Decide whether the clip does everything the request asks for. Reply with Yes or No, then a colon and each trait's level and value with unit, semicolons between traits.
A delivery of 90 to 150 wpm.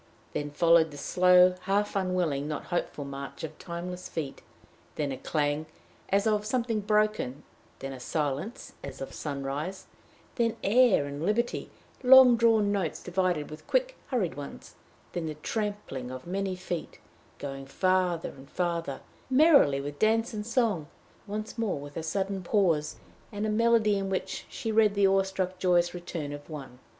No: average, 160 wpm